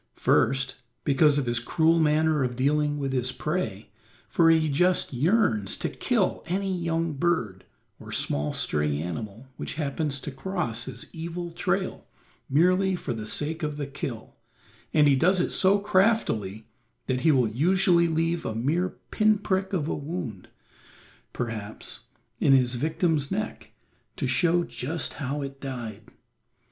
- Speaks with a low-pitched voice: No, medium, 150 Hz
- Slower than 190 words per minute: Yes, average, 150 wpm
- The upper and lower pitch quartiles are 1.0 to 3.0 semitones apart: No, wide, 5.6 semitones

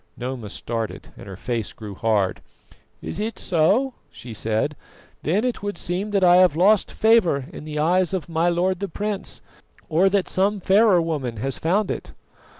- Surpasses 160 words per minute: Yes, average, 175 wpm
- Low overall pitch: No, medium, 175 Hz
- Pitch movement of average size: No, wide, 7.3 semitones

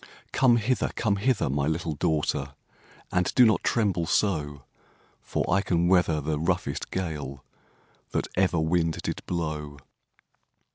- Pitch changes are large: No, average, 4.1 semitones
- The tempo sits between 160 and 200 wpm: No, slow, 135 wpm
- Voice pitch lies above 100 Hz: No, very low, 85 Hz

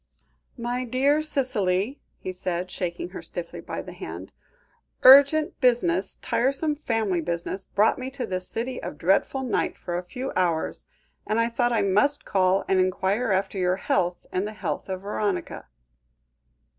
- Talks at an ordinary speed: Yes, average, 155 wpm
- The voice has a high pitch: Yes, high, 205 Hz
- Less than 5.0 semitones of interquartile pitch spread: No, wide, 5.6 semitones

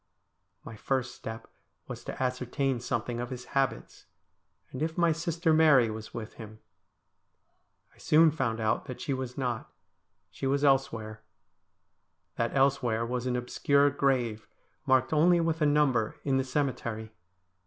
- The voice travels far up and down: No, average, 3.4 semitones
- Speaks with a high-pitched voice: No, low, 130 Hz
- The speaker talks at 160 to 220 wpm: No, average, 145 wpm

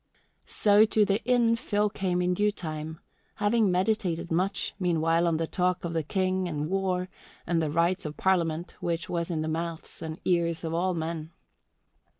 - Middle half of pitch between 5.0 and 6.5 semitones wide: No, average, 2.7 semitones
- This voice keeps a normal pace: Yes, average, 175 wpm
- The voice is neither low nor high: Yes, medium, 175 Hz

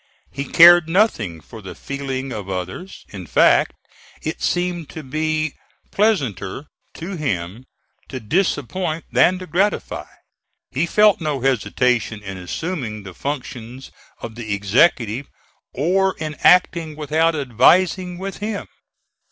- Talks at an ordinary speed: No, slow, 125 wpm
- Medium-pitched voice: Yes, medium, 145 Hz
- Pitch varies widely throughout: Yes, wide, 7.3 semitones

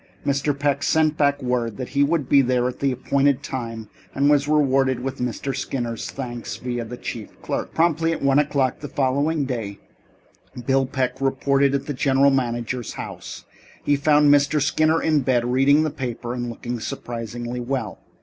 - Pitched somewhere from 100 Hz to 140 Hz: Yes, low, 135 Hz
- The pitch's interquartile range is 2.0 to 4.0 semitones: Yes, narrow, 2.6 semitones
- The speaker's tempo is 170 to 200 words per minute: Yes, average, 175 wpm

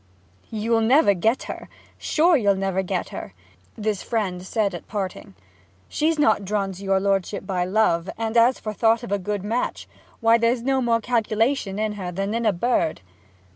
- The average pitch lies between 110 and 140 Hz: No, high, 215 Hz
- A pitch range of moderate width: Yes, average, 3.2 semitones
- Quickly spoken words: No, average, 185 wpm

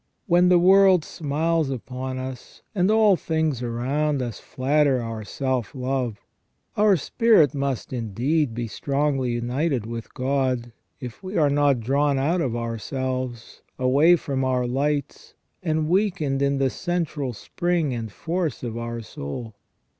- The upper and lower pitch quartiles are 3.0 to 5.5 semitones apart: Yes, average, 4.4 semitones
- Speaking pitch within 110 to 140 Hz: Yes, low, 135 Hz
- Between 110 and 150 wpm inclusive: Yes, average, 140 wpm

